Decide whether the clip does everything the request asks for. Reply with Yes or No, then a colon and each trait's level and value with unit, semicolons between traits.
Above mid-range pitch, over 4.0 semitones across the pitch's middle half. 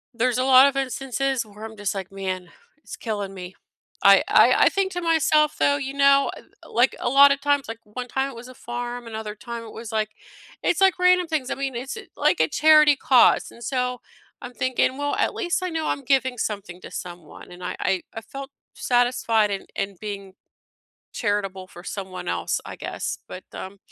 Yes: high, 245 Hz; average, 4.9 semitones